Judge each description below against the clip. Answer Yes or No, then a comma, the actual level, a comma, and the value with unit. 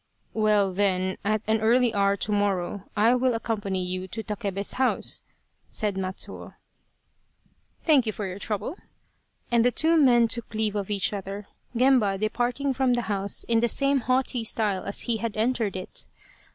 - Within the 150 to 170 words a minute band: No, average, 180 wpm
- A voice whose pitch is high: Yes, high, 215 Hz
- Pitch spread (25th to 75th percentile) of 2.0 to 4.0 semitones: Yes, average, 3.3 semitones